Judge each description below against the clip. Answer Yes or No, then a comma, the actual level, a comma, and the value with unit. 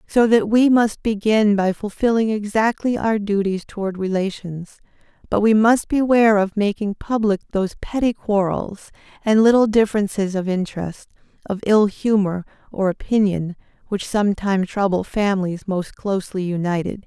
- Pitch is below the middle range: No, high, 205 Hz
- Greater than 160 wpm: No, slow, 135 wpm